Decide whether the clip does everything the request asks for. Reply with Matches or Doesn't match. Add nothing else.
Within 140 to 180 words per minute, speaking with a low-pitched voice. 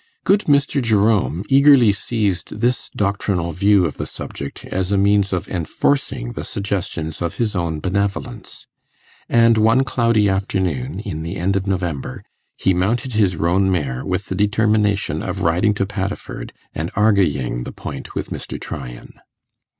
Matches